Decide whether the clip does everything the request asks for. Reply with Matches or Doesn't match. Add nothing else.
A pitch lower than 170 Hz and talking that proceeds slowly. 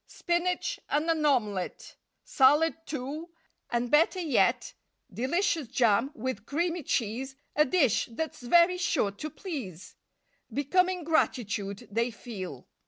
Doesn't match